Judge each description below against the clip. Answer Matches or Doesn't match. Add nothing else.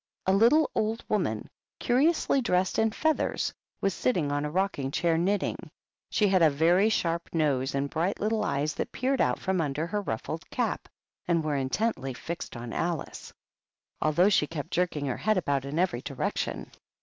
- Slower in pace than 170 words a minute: Doesn't match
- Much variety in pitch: Matches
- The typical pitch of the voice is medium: Matches